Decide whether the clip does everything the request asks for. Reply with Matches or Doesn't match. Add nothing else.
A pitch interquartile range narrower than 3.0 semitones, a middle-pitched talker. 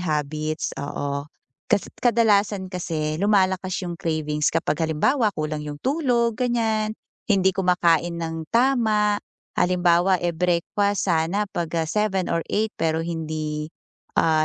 Doesn't match